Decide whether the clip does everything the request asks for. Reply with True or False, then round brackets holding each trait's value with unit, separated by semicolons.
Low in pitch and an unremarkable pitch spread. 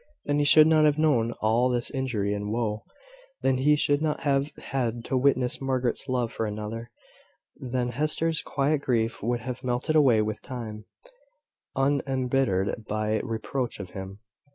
True (125 Hz; 3.8 semitones)